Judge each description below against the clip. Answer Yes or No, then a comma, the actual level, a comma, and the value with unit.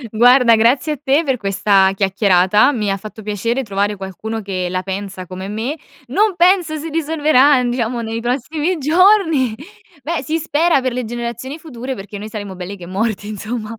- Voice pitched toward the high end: Yes, high, 235 Hz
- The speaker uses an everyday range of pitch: No, wide, 6.1 semitones